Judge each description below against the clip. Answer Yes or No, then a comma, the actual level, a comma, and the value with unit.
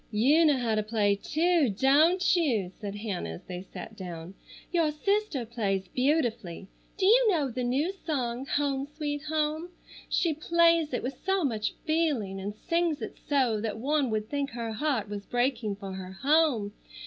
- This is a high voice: Yes, very high, 260 Hz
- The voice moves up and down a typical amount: No, wide, 6.6 semitones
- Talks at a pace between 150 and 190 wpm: Yes, average, 170 wpm